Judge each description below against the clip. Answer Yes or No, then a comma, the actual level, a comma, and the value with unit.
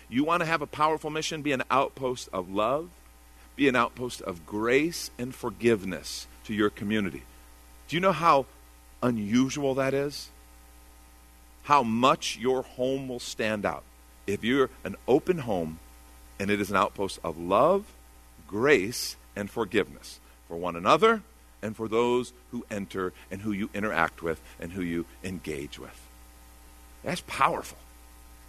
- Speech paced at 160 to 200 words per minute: No, average, 150 wpm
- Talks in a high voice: No, very low, 95 Hz